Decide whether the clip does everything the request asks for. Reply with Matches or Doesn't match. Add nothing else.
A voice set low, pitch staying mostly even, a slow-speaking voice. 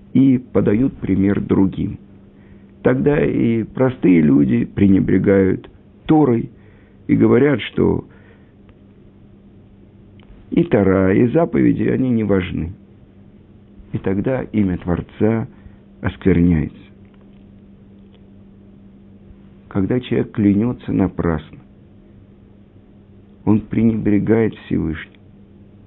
Matches